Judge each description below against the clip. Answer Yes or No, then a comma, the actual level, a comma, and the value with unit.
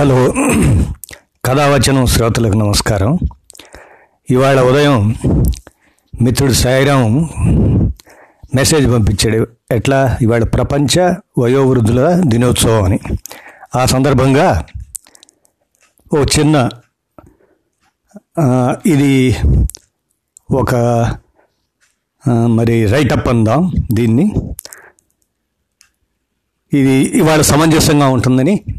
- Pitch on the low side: Yes, low, 125 Hz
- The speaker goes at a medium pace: No, slow, 65 wpm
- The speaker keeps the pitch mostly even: No, average, 3.5 semitones